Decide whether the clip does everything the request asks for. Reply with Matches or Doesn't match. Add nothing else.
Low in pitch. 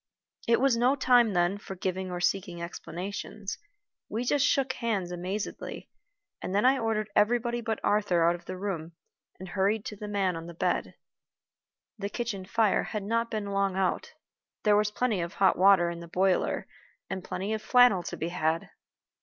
Doesn't match